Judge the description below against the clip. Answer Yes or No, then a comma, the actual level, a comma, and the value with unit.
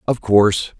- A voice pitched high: No, low, 105 Hz